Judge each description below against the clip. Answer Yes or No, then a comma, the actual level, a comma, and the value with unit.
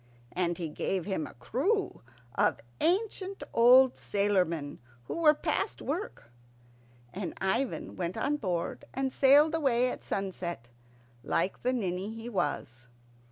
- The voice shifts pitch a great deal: Yes, wide, 7.4 semitones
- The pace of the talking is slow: Yes, slow, 130 wpm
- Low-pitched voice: No, high, 215 Hz